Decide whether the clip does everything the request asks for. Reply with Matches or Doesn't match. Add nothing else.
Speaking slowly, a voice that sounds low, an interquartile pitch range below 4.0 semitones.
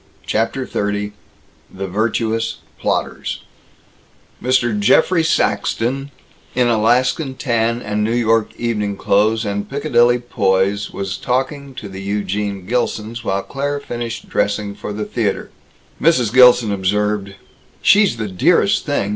Matches